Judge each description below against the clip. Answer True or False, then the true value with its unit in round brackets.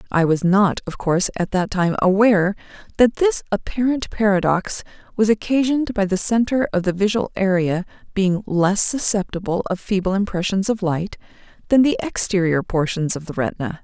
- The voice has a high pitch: True (195 Hz)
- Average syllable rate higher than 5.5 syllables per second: False (5.2 syllables/s)